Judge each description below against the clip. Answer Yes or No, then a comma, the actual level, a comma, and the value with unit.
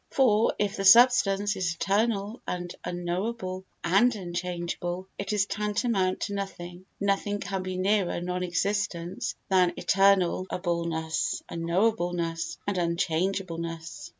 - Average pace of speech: No, slow, 110 wpm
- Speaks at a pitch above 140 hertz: Yes, medium, 185 Hz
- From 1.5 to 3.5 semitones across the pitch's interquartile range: Yes, narrow, 2.6 semitones